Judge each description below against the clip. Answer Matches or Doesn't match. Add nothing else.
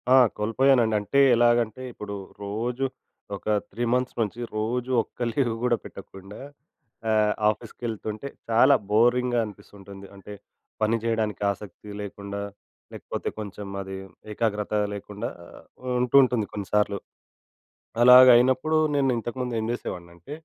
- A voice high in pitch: Doesn't match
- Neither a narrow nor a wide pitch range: Matches